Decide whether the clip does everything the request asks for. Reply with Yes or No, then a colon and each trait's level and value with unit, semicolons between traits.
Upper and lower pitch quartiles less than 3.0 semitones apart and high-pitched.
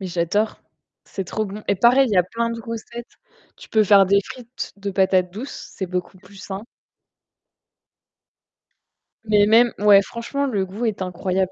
No: average, 3.3 semitones; high, 205 Hz